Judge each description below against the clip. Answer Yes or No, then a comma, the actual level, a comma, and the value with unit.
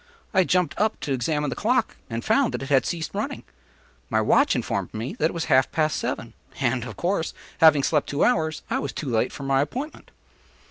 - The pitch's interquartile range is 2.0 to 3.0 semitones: No, average, 5.1 semitones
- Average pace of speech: No, fast, 215 wpm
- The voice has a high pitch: No, medium, 155 Hz